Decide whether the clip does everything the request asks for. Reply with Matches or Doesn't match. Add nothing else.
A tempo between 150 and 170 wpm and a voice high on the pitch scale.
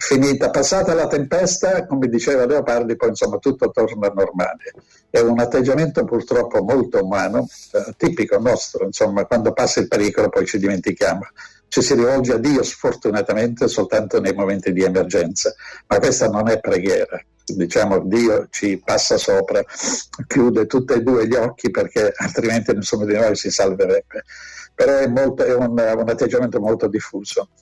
Matches